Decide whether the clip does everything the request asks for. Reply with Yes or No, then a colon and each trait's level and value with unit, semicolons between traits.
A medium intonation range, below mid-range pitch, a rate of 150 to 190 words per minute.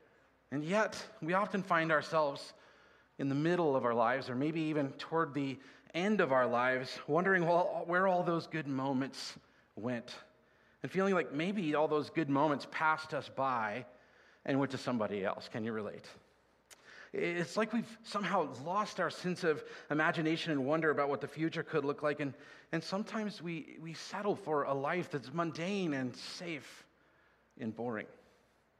No: average, 4.1 semitones; medium, 155 Hz; average, 165 wpm